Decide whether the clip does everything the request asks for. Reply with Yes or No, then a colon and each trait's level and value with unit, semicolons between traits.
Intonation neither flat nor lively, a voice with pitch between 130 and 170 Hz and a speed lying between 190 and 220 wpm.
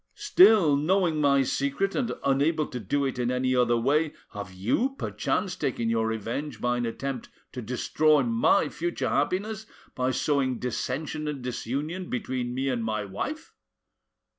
No: average, 4.1 semitones; low, 135 Hz; average, 155 wpm